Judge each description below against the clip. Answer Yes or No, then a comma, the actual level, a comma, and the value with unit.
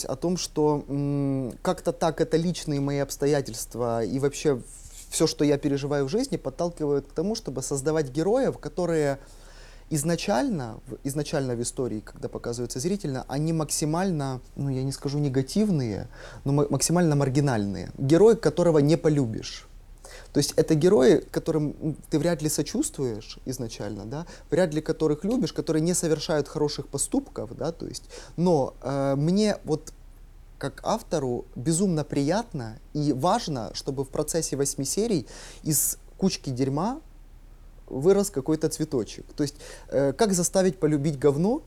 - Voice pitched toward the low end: No, medium, 150 Hz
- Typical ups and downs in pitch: Yes, average, 3.2 semitones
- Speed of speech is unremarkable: Yes, average, 140 wpm